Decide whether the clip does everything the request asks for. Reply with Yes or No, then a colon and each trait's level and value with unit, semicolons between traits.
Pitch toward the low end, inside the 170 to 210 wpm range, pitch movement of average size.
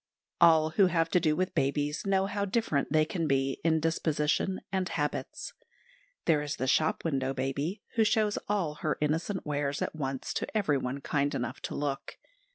No: medium, 155 Hz; average, 175 wpm; average, 4.3 semitones